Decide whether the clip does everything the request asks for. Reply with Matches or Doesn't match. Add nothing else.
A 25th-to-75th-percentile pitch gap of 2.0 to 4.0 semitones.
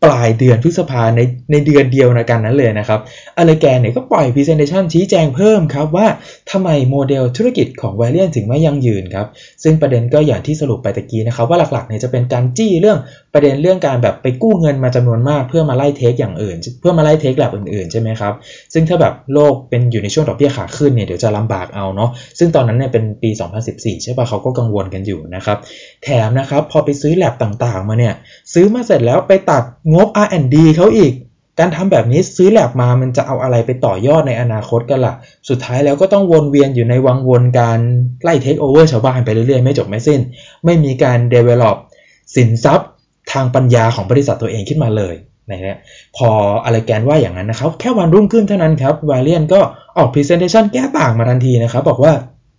Doesn't match